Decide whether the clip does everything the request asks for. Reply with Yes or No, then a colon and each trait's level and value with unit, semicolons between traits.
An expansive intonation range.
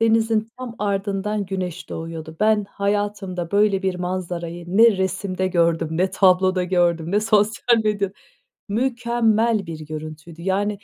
No: average, 3.3 semitones